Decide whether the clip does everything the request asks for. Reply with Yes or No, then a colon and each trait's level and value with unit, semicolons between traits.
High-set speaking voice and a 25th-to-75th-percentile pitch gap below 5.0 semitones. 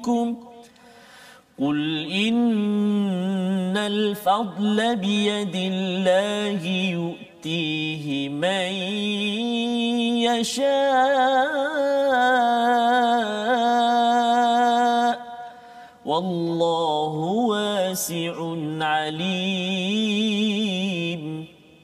Yes: high, 210 Hz; average, 4.6 semitones